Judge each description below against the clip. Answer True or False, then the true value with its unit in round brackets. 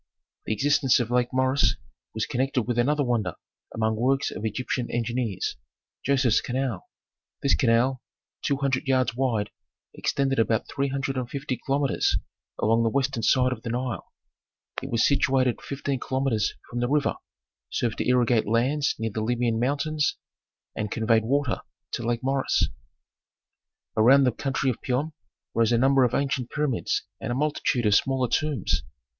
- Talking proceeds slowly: False (155 wpm)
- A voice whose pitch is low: True (125 Hz)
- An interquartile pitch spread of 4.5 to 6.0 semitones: False (2.8 semitones)